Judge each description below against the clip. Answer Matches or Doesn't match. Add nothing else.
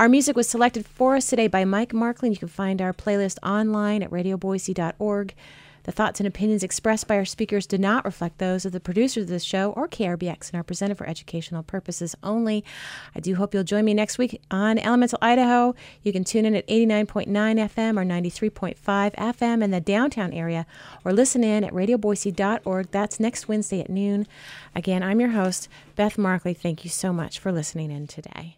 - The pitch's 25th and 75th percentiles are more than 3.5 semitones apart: Doesn't match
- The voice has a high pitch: Matches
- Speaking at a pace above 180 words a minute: Matches